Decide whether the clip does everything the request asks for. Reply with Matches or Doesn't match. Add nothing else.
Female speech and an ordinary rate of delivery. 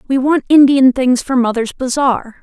Matches